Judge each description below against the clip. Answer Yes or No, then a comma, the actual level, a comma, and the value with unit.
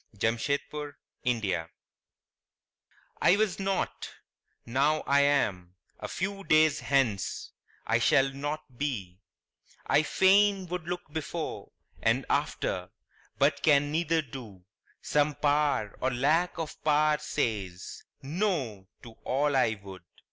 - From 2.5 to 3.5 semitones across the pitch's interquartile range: No, average, 4.8 semitones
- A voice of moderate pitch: Yes, medium, 145 Hz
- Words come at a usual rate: No, slow, 115 wpm